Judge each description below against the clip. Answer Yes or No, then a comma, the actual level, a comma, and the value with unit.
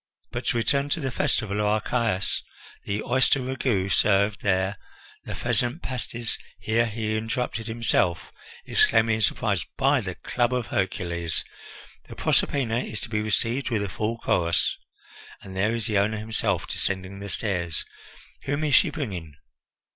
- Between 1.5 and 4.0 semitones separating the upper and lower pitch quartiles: Yes, average, 3.4 semitones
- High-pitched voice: No, low, 110 Hz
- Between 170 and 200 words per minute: No, average, 155 wpm